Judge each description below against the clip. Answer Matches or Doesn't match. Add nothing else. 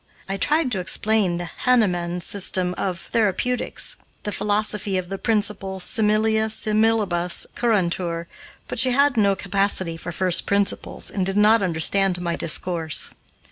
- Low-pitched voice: Doesn't match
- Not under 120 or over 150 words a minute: Matches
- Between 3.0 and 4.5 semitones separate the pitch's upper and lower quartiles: Matches